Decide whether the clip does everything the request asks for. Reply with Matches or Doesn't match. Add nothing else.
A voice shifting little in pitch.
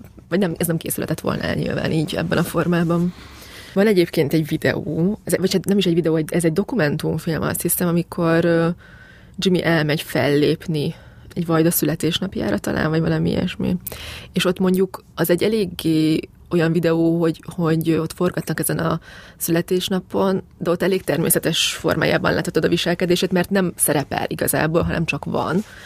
Matches